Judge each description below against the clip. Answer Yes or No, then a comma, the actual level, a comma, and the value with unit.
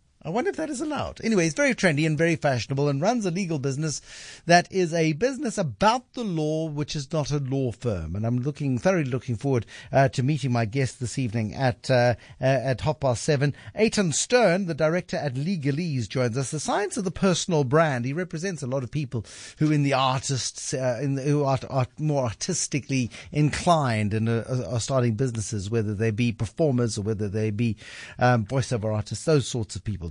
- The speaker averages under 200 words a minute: No, fast, 205 wpm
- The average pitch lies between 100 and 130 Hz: No, medium, 140 Hz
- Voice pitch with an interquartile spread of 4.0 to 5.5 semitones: Yes, average, 4.8 semitones